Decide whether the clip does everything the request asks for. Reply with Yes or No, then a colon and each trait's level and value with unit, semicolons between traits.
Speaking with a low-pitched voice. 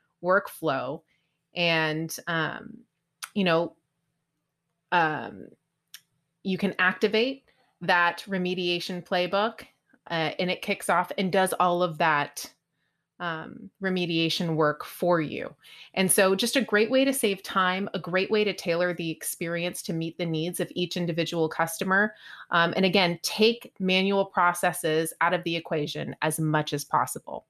No: medium, 180 Hz